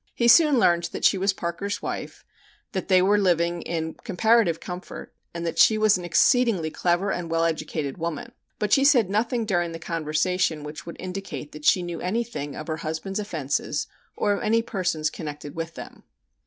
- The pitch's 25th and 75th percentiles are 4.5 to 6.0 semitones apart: No, average, 4.0 semitones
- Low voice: No, medium, 175 Hz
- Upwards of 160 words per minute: Yes, average, 185 wpm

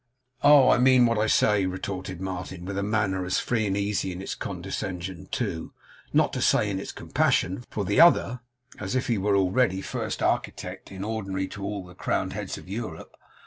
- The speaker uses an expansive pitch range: No, average, 2.7 semitones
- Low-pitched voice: Yes, low, 100 Hz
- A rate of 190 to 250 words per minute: Yes, average, 195 wpm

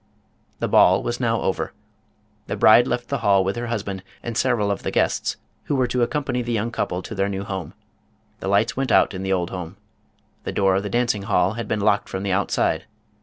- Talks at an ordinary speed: No, fast, 220 wpm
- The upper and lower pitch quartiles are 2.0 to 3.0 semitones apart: No, average, 3.6 semitones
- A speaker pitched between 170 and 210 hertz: No, low, 105 Hz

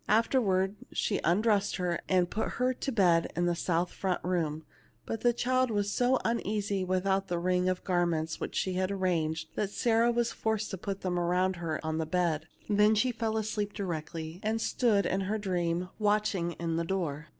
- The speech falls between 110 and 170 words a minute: No, average, 195 wpm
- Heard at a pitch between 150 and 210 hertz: Yes, high, 190 Hz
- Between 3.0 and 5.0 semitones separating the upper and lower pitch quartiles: Yes, average, 3.6 semitones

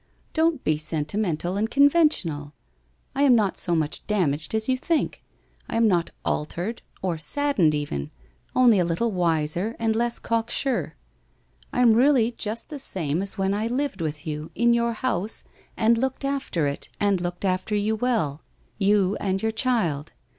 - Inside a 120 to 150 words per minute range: No, average, 170 wpm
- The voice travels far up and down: Yes, wide, 6.1 semitones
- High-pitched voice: Yes, high, 210 Hz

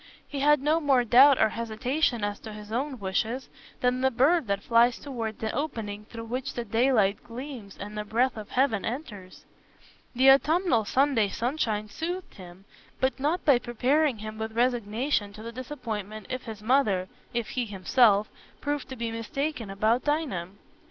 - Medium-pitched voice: No, high, 235 Hz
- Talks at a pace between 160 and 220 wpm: Yes, average, 165 wpm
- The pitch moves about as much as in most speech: Yes, average, 4.1 semitones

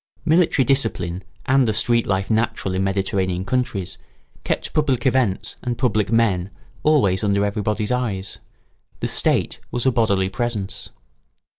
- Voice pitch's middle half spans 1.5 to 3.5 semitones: No, average, 4.4 semitones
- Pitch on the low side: Yes, low, 105 Hz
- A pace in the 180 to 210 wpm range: No, slow, 135 wpm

